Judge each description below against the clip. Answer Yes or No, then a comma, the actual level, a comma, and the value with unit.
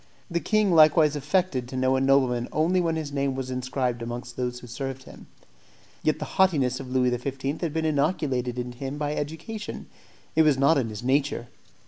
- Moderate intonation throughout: Yes, average, 3.6 semitones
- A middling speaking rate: Yes, average, 190 wpm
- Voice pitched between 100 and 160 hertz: Yes, low, 135 Hz